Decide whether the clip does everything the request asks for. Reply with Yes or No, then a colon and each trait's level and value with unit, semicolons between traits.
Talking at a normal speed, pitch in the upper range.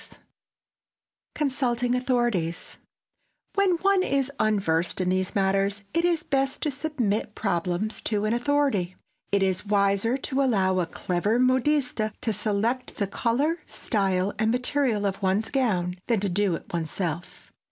Yes: average, 145 wpm; high, 215 Hz